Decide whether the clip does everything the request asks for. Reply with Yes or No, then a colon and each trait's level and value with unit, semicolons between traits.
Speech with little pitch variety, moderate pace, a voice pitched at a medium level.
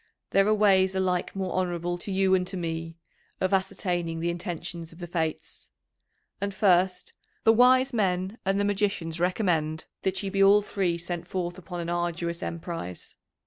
Yes: narrow, 2.3 semitones; average, 170 wpm; medium, 180 Hz